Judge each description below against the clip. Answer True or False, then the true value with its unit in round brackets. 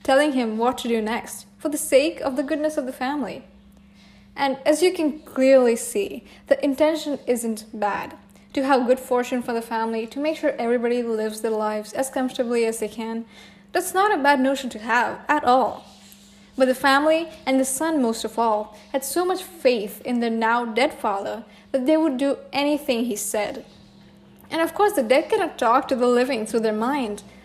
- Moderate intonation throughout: True (4.1 semitones)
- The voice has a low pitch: False (255 Hz)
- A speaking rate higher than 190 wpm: True (200 wpm)